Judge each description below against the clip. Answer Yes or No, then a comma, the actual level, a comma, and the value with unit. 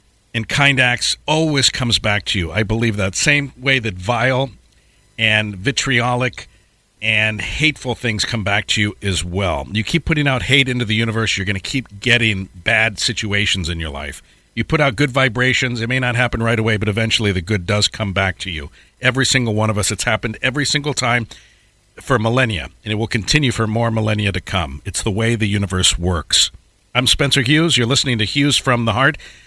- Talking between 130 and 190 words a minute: No, fast, 205 wpm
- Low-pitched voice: Yes, low, 110 Hz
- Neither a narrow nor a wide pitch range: Yes, average, 3.7 semitones